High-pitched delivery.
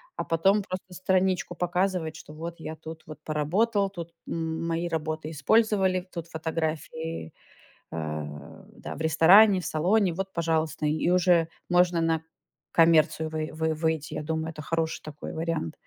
No: medium, 165 Hz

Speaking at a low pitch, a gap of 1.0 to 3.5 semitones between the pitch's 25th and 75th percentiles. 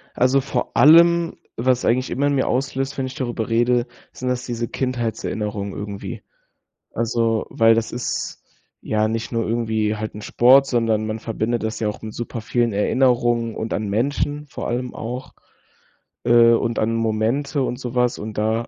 Yes: low, 120 Hz; narrow, 2.5 semitones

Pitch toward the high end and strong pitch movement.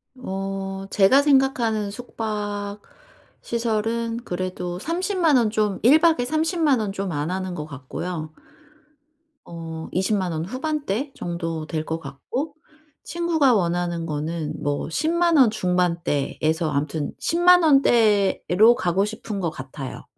Yes: high, 200 Hz; wide, 7.0 semitones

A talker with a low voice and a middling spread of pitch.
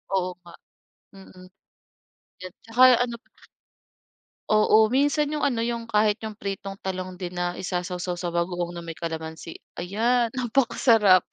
No: high, 195 Hz; average, 4.6 semitones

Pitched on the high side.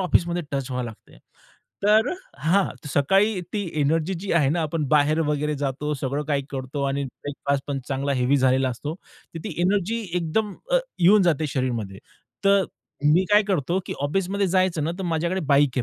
No: medium, 150 Hz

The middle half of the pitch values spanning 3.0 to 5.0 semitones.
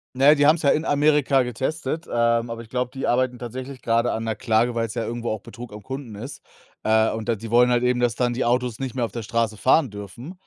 No: narrow, 2.4 semitones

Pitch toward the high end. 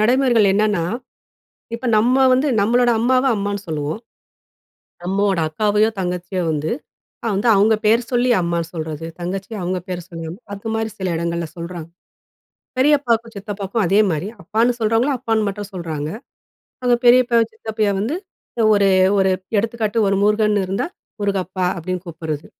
Yes: high, 205 Hz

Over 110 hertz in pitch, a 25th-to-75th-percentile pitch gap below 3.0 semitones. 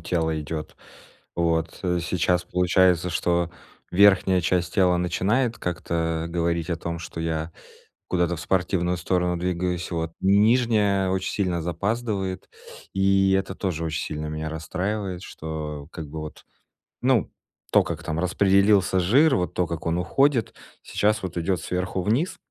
No: very low, 90 Hz; narrow, 2.6 semitones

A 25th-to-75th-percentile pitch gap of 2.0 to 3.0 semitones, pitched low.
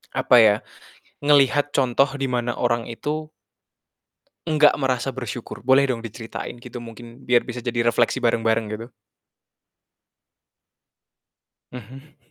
Yes: narrow, 2.5 semitones; low, 125 Hz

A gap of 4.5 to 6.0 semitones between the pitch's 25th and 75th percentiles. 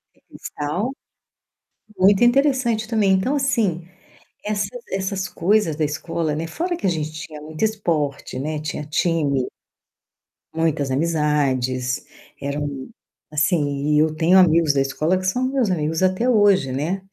Yes: average, 5.2 semitones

